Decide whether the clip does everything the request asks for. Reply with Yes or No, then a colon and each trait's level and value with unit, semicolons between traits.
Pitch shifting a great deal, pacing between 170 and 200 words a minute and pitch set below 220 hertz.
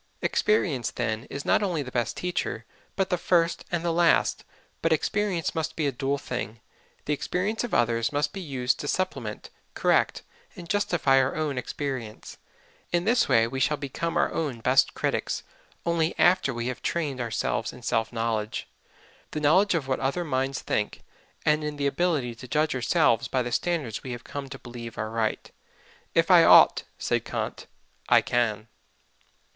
Yes: wide, 5.7 semitones; average, 175 wpm; medium, 140 Hz